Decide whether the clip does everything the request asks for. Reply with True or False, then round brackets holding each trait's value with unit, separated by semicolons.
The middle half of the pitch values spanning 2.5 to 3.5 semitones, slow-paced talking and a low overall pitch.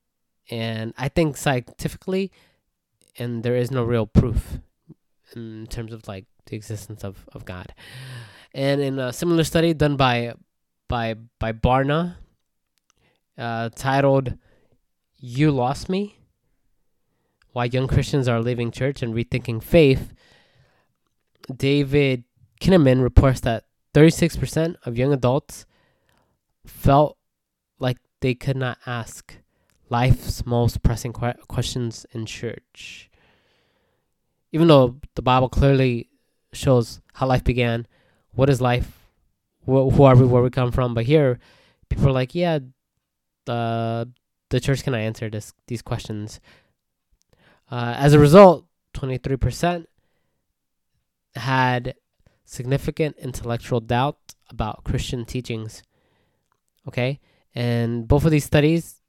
True (2.9 semitones; 120 wpm; 125 Hz)